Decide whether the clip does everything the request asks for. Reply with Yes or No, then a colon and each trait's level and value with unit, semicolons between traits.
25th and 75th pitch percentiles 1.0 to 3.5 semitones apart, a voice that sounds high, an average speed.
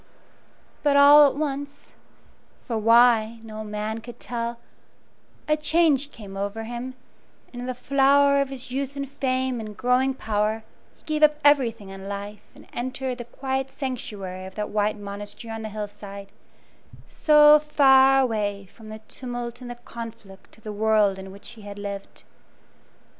No: average, 4.2 semitones; high, 235 Hz; average, 165 wpm